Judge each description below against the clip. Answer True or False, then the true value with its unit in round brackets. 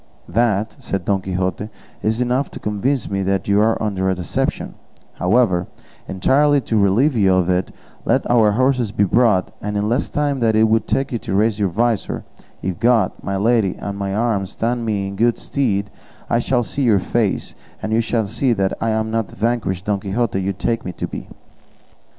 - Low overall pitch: True (110 Hz)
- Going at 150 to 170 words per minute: False (200 wpm)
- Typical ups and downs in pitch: True (3.4 semitones)